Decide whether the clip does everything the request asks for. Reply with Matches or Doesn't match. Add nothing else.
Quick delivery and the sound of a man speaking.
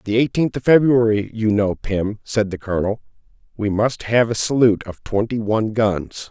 Doesn't match